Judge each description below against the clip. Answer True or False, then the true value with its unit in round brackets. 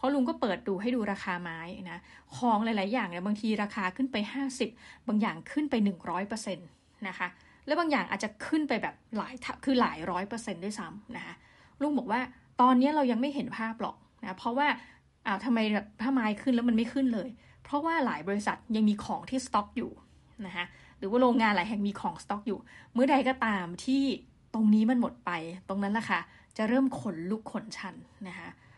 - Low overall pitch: False (225 Hz)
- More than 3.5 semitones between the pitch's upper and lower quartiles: True (4.4 semitones)